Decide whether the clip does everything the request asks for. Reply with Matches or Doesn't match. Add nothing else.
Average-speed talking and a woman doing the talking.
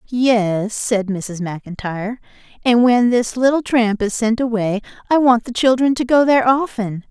Matches